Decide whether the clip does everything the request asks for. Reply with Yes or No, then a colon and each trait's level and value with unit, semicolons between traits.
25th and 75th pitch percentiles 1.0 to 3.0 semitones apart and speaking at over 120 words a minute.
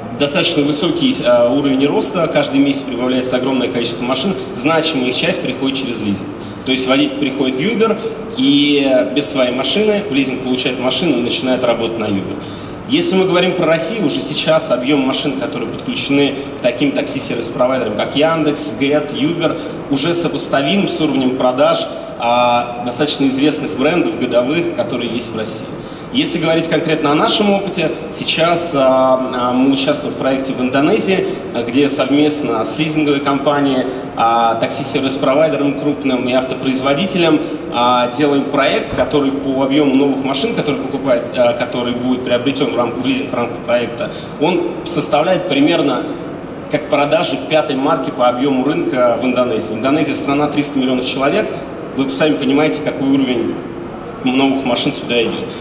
No: average, 3.4 semitones; average, 145 wpm